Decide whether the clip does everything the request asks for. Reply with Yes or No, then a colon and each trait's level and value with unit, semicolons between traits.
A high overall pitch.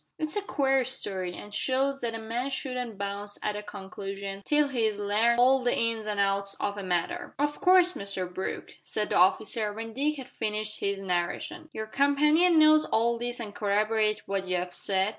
Yes: high, 220 Hz